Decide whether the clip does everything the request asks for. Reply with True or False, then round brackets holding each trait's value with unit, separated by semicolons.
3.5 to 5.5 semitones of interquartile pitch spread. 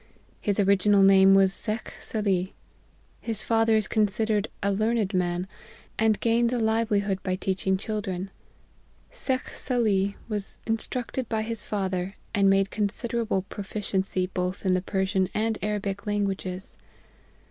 False (2.4 semitones)